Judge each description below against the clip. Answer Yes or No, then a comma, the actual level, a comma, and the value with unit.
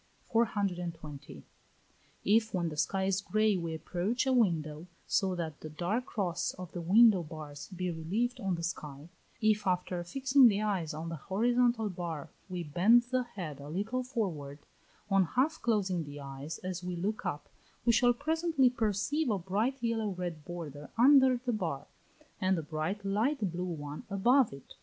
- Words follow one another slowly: No, average, 170 wpm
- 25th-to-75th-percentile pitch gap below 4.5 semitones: No, wide, 5.6 semitones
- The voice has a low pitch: No, medium, 185 Hz